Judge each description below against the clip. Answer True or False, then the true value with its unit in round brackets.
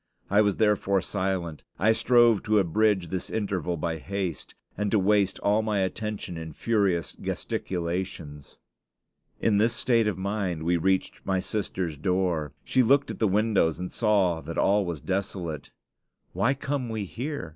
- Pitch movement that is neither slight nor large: True (3.6 semitones)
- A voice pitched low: True (95 Hz)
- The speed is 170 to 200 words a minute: False (155 wpm)